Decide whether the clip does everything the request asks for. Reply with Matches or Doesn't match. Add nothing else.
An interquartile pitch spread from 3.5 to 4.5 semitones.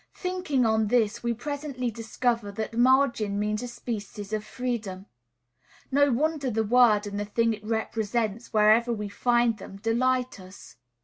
Doesn't match